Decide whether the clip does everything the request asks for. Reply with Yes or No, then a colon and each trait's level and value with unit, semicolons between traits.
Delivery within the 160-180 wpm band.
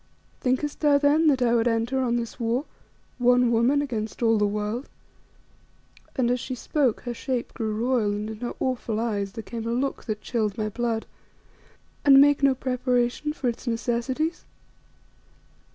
Yes: average, 170 wpm